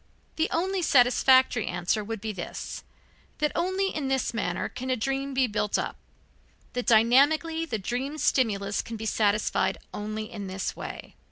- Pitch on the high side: Yes, high, 245 Hz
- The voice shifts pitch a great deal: No, average, 4.6 semitones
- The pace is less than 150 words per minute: No, average, 160 wpm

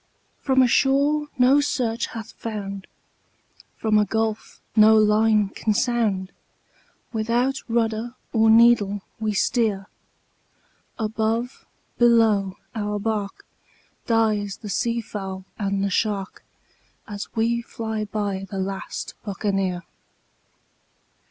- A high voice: Yes, high, 220 Hz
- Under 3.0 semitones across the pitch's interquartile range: Yes, narrow, 2.5 semitones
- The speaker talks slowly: Yes, slow, 105 wpm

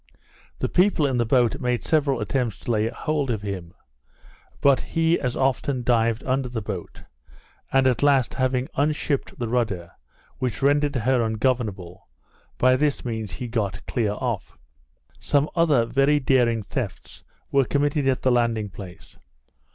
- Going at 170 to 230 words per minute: No, average, 150 wpm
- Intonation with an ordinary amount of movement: Yes, average, 3.6 semitones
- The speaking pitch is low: Yes, low, 125 Hz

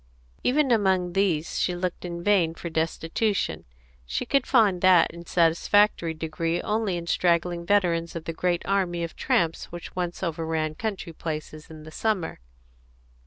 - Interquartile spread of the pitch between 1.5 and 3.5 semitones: Yes, average, 2.9 semitones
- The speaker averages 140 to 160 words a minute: Yes, average, 155 wpm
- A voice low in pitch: No, medium, 175 Hz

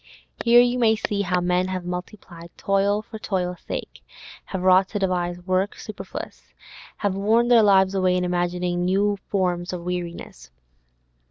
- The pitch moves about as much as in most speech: No, narrow, 2.2 semitones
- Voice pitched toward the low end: No, medium, 185 Hz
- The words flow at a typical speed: Yes, average, 155 wpm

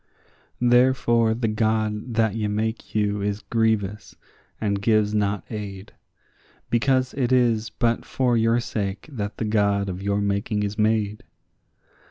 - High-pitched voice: No, low, 110 Hz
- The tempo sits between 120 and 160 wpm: Yes, average, 140 wpm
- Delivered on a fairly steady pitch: Yes, narrow, 2.1 semitones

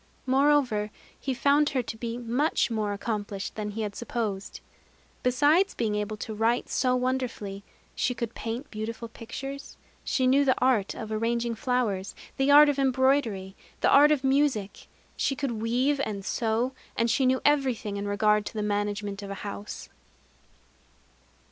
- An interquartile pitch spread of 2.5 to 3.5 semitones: No, average, 4.0 semitones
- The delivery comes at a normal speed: Yes, average, 160 wpm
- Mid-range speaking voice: No, high, 235 Hz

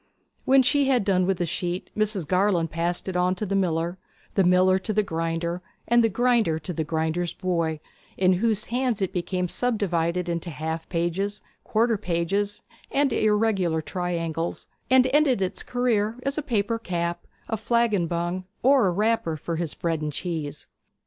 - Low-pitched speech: No, medium, 185 Hz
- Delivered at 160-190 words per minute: Yes, average, 170 wpm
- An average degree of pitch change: Yes, average, 4.2 semitones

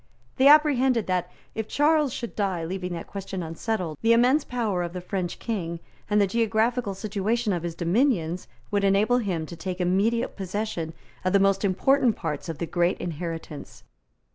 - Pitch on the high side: Yes, high, 195 Hz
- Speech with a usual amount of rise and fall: Yes, average, 4.7 semitones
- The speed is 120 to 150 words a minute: No, average, 170 wpm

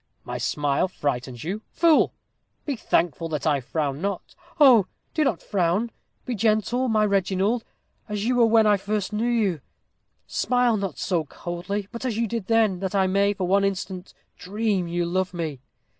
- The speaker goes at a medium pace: Yes, average, 175 wpm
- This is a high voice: Yes, high, 195 Hz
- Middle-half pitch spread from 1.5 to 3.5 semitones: No, average, 4.3 semitones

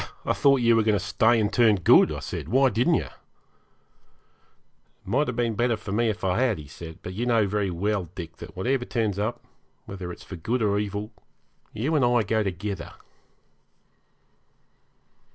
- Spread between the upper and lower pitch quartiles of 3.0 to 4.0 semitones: Yes, average, 3.7 semitones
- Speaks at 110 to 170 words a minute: No, average, 190 wpm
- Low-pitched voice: Yes, low, 105 Hz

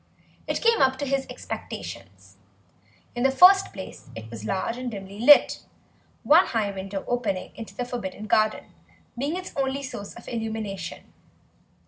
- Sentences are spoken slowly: No, average, 155 wpm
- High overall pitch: Yes, high, 235 Hz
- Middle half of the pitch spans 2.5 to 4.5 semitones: No, average, 5.1 semitones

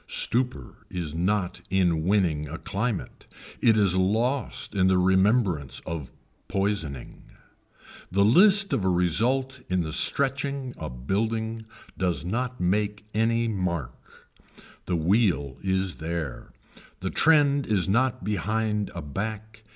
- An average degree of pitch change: Yes, average, 4.5 semitones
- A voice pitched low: Yes, low, 100 Hz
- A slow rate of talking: Yes, slow, 120 wpm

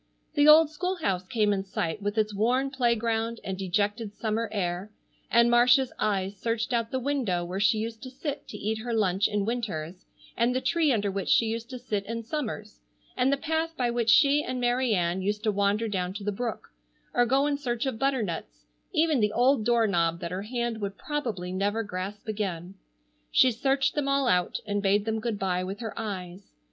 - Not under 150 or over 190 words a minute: No, fast, 205 wpm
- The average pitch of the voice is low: No, high, 220 Hz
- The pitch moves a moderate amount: Yes, average, 4.0 semitones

